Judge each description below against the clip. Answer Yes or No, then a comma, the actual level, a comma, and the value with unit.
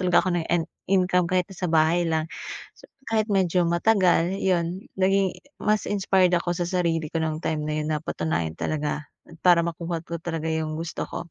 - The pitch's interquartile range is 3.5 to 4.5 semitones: No, narrow, 2.4 semitones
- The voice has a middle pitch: Yes, medium, 170 Hz